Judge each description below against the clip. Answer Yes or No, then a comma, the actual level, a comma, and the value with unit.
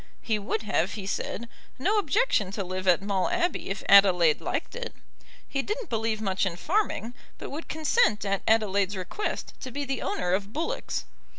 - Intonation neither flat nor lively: No, wide, 7.7 semitones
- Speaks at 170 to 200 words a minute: Yes, average, 180 wpm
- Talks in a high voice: Yes, high, 215 Hz